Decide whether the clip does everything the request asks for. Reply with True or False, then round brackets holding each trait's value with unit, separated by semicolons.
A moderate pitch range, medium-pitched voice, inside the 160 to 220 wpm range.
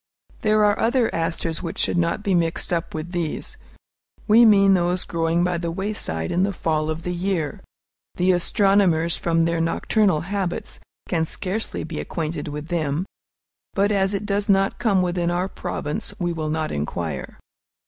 True (3.2 semitones; 175 Hz; 170 wpm)